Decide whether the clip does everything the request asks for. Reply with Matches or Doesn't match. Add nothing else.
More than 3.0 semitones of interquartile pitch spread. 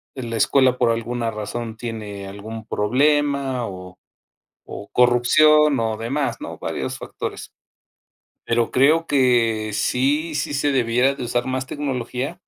Matches